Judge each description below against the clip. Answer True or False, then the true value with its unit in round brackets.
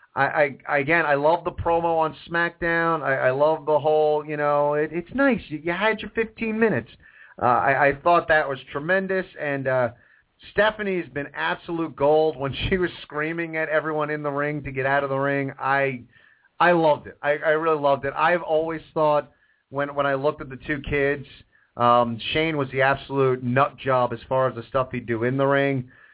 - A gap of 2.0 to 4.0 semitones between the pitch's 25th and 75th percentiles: True (3.0 semitones)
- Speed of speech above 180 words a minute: True (205 wpm)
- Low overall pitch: False (145 Hz)